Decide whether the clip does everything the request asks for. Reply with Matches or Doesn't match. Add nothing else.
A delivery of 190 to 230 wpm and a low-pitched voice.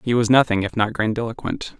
Matches